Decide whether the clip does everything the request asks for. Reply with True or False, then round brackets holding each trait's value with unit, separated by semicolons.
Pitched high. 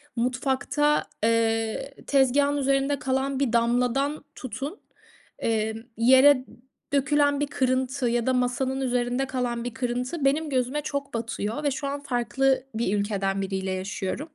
True (255 Hz)